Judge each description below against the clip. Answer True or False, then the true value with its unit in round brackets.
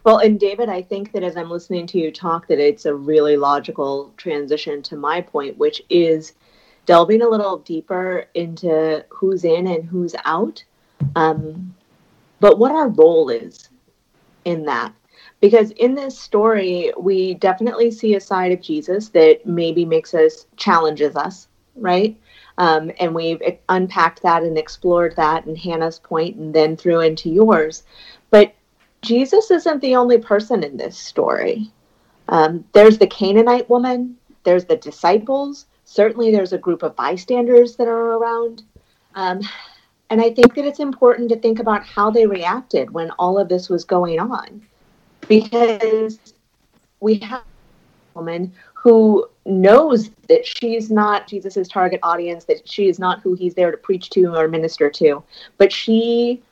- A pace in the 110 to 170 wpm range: True (160 wpm)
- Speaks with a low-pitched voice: False (195 Hz)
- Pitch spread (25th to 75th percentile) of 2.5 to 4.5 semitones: False (5.4 semitones)